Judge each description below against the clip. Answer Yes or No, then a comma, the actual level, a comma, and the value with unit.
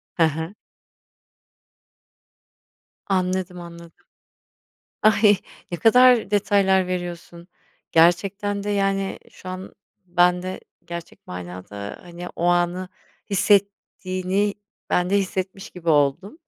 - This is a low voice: No, medium, 185 Hz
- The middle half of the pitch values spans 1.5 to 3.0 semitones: Yes, narrow, 2.5 semitones